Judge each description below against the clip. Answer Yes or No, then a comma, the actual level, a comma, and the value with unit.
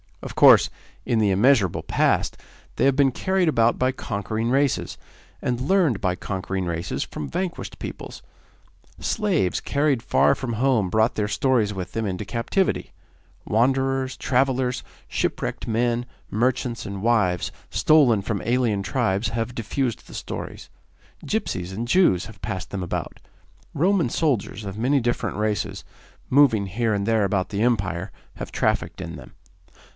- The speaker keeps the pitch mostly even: No, average, 4.8 semitones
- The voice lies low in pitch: Yes, low, 115 Hz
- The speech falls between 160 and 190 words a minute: No, average, 145 wpm